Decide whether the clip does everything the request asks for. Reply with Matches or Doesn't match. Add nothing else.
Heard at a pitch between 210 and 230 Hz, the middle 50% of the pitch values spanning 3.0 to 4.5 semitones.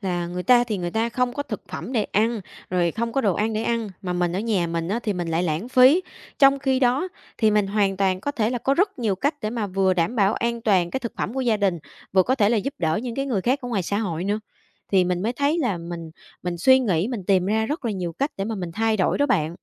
Doesn't match